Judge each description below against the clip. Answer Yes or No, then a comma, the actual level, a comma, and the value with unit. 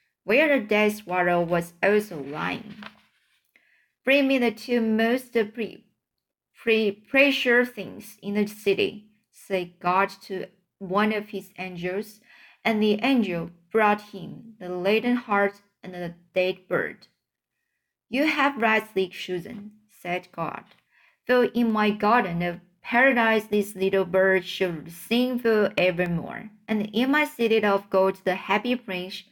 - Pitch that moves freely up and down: No, average, 3.4 semitones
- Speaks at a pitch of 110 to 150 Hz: No, high, 210 Hz